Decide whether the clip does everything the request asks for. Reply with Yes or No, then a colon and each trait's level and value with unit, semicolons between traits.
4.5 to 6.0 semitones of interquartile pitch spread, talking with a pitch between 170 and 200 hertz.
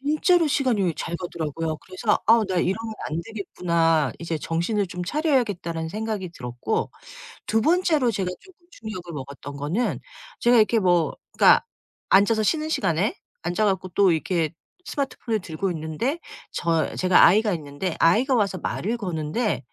Yes: wide, 5.4 semitones; high, 190 Hz